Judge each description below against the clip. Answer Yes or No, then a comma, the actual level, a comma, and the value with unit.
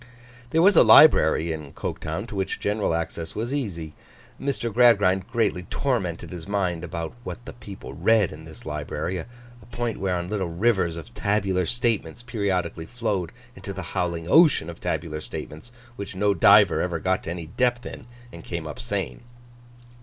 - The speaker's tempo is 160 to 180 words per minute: Yes, average, 170 wpm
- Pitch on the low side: Yes, very low, 95 Hz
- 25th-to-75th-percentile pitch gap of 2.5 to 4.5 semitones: No, average, 5.0 semitones